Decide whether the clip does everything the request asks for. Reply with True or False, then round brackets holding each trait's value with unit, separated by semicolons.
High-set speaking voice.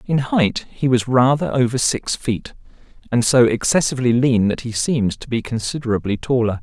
False (120 Hz)